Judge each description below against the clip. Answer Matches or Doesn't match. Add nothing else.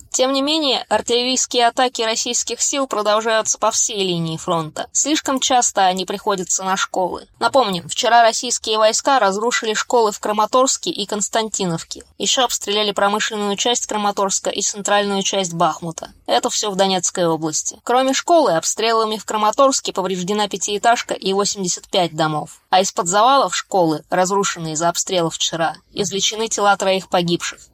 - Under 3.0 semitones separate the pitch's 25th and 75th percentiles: Doesn't match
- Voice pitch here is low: Doesn't match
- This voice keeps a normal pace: Matches